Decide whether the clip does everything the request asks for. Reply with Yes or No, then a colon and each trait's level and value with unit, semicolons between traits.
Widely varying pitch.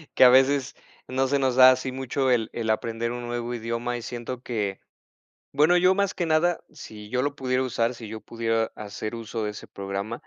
No: average, 2.7 semitones